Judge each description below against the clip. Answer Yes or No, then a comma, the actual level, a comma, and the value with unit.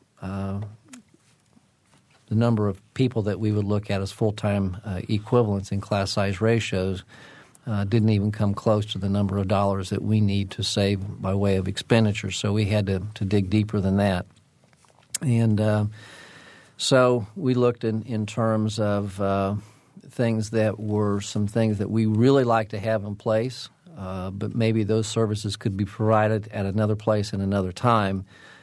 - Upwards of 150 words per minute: Yes, average, 175 wpm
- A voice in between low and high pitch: No, low, 105 Hz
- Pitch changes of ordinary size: No, narrow, 2.0 semitones